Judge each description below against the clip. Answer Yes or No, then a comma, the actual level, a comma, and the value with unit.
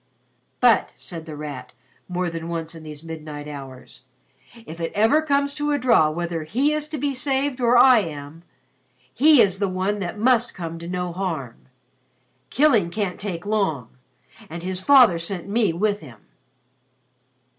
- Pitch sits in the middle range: Yes, medium, 180 Hz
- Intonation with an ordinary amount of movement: No, wide, 6.7 semitones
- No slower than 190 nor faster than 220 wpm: No, average, 165 wpm